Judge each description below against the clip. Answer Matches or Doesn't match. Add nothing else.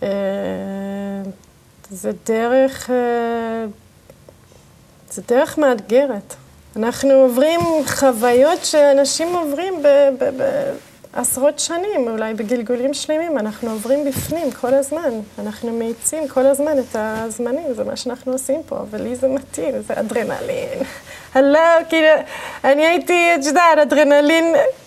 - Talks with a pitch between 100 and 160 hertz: Doesn't match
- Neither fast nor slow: Matches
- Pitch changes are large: Doesn't match